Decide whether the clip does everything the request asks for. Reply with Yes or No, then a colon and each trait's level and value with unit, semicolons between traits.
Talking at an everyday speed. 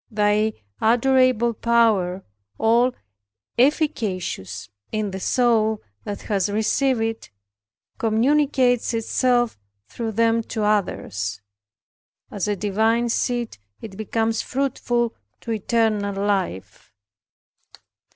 No: slow, 95 wpm